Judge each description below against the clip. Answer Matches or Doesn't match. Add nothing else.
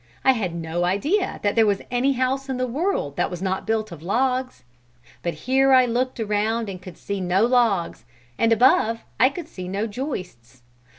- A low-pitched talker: Doesn't match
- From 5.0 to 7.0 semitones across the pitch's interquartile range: Matches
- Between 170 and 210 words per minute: Matches